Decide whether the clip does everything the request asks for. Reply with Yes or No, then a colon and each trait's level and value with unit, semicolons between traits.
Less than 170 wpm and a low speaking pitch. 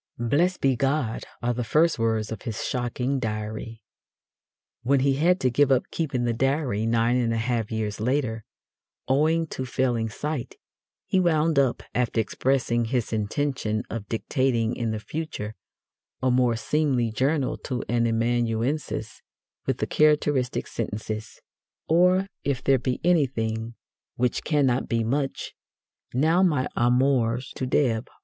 Yes: average, 140 wpm; low, 125 Hz